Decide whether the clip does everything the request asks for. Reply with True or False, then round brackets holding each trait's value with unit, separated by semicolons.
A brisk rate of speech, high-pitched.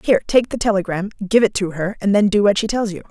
True (290 wpm; 205 Hz)